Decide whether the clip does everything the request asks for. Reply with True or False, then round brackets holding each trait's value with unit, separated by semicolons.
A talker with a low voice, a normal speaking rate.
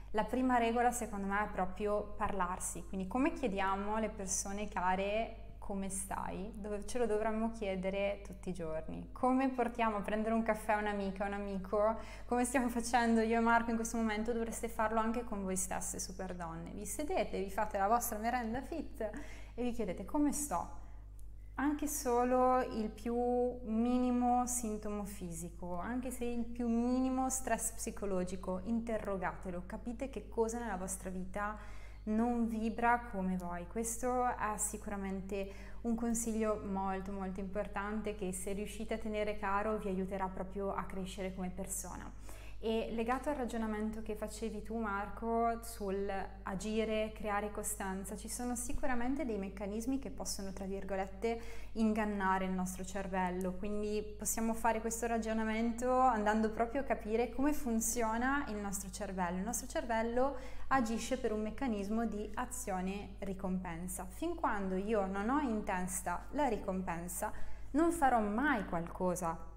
False (215 Hz; 150 wpm)